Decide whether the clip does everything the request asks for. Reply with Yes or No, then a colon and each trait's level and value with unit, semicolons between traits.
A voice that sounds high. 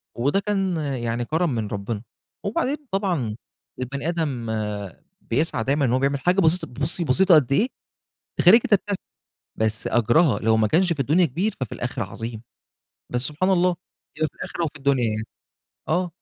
No: medium, 145 Hz